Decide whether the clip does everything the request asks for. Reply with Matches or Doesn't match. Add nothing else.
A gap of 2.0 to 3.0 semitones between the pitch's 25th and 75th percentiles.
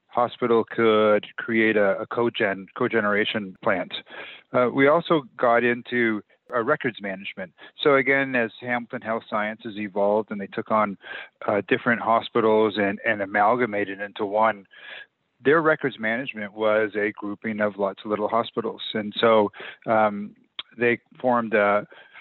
Matches